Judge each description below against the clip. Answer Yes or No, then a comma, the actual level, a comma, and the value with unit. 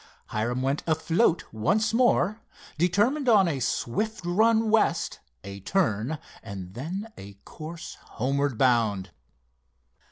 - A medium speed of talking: No, slow, 115 wpm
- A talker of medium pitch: Yes, medium, 160 Hz